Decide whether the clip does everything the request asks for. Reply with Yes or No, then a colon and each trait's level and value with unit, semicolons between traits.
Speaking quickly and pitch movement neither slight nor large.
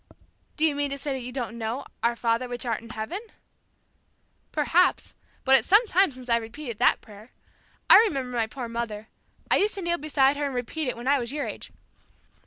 Yes: fast, 210 wpm; average, 3.9 semitones